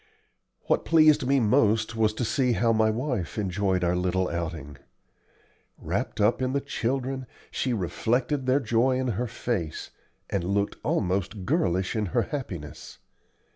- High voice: No, low, 110 Hz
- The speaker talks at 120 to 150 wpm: Yes, average, 145 wpm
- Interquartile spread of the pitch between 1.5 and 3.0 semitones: No, wide, 5.6 semitones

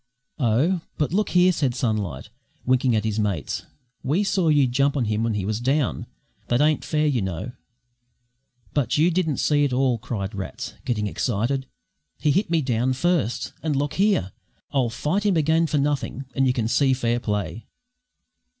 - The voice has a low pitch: Yes, low, 130 Hz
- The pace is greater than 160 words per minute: Yes, average, 175 wpm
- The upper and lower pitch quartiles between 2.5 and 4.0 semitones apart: No, average, 5.3 semitones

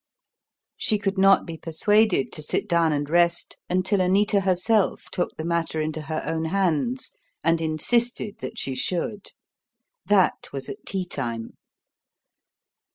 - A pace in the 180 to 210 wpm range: No, average, 140 wpm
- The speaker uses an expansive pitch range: No, average, 4.0 semitones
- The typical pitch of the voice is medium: Yes, medium, 175 Hz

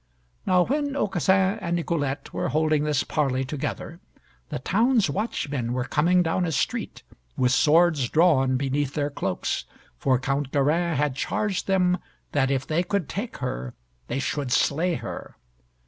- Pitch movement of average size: Yes, average, 5.0 semitones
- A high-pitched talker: No, medium, 150 Hz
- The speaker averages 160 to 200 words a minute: No, average, 150 wpm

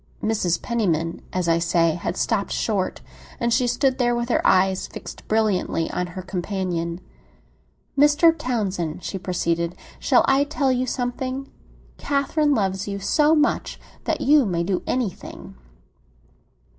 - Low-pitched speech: No, high, 205 Hz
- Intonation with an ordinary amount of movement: No, wide, 6.4 semitones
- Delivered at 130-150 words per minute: Yes, average, 140 wpm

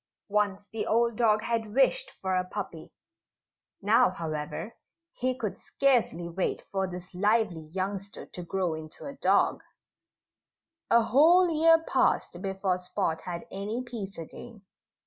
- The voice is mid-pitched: No, high, 205 Hz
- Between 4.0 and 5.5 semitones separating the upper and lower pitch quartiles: Yes, average, 4.4 semitones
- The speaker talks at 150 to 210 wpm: No, slow, 135 wpm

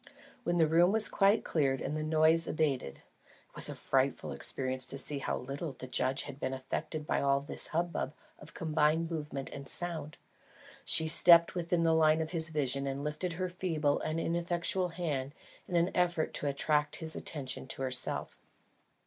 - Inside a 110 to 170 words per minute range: No, average, 180 wpm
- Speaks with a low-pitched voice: No, medium, 155 Hz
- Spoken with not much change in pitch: No, average, 3.4 semitones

